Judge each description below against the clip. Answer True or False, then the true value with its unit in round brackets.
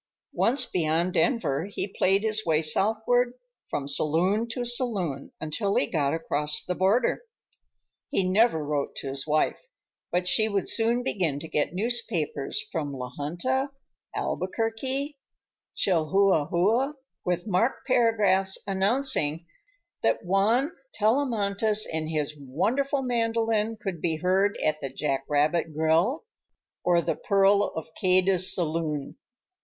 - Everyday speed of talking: False (125 wpm)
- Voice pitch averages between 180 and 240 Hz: True (190 Hz)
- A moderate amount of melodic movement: False (6.2 semitones)